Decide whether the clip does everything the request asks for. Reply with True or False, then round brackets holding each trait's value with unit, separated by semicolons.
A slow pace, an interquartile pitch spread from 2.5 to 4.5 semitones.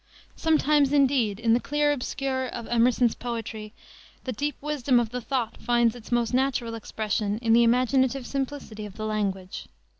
False (160 wpm; 3.2 semitones)